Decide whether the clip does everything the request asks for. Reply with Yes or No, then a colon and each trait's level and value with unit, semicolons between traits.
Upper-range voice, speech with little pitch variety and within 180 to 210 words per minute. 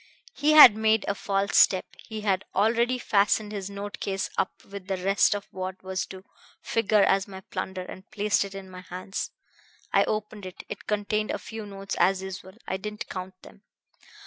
Yes: high, 195 Hz; narrow, 1.9 semitones; average, 190 wpm